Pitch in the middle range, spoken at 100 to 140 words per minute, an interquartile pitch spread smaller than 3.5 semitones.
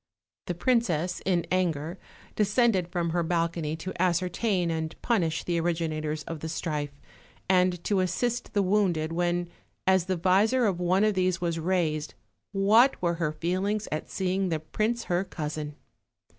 No: medium, 175 Hz; average, 155 wpm; average, 2.7 semitones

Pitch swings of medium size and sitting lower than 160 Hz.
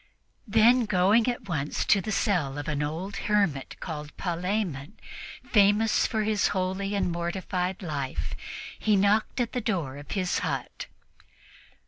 No: average, 4.5 semitones; high, 190 Hz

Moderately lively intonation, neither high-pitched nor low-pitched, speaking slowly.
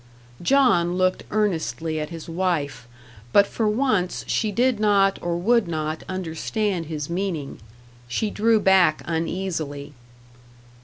Yes: average, 4.5 semitones; medium, 180 Hz; slow, 120 wpm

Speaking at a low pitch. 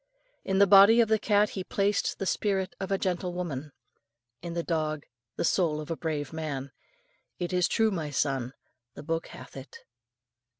No: medium, 175 Hz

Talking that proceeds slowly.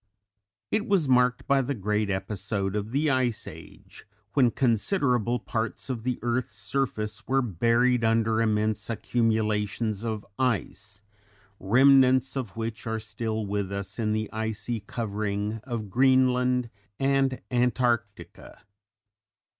Yes: slow, 120 wpm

